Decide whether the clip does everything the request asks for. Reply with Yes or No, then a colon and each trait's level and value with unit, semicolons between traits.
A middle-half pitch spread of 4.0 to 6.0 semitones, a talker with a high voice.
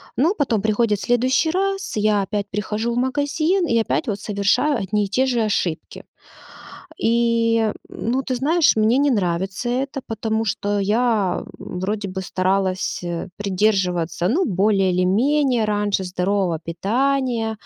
Yes: average, 4.4 semitones; high, 215 Hz